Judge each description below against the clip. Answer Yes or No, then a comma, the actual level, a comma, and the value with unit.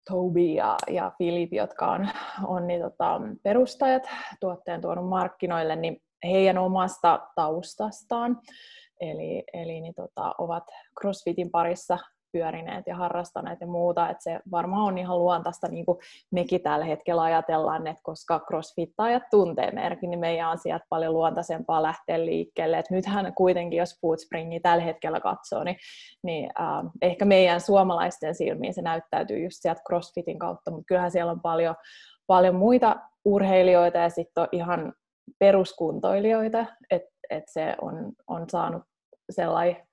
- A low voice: No, medium, 175 Hz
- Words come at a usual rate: Yes, average, 140 wpm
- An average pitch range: No, narrow, 2.2 semitones